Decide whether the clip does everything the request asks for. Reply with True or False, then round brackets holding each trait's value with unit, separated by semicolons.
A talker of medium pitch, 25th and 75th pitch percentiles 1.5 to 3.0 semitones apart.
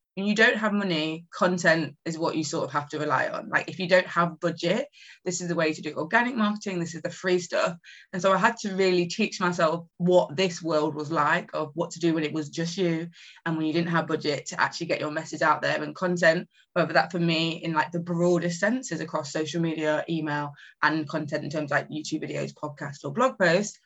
True (170 Hz; 2.7 semitones)